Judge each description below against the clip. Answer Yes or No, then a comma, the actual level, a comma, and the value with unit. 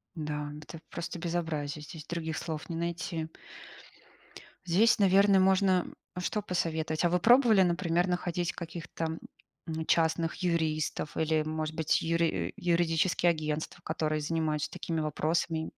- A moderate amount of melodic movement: No, narrow, 1.9 semitones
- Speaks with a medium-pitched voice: Yes, medium, 165 Hz